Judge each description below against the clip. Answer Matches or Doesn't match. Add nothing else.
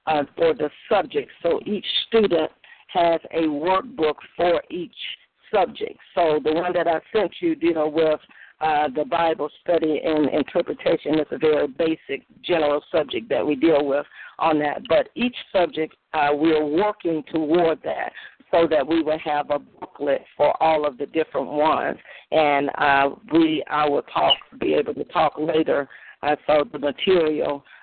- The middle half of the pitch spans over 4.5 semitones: Doesn't match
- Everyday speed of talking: Matches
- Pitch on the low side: Doesn't match